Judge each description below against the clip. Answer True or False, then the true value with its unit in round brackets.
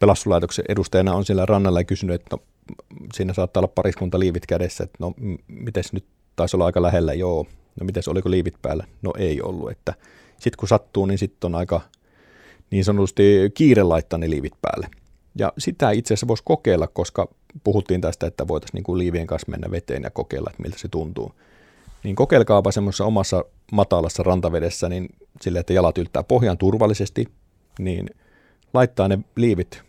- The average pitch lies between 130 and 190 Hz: False (95 Hz)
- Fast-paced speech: True (170 wpm)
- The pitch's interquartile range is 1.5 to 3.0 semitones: True (2.4 semitones)